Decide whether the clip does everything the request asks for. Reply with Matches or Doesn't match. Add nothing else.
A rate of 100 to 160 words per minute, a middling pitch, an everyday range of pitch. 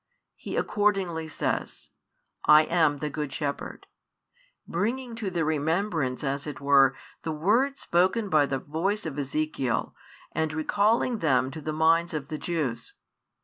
Matches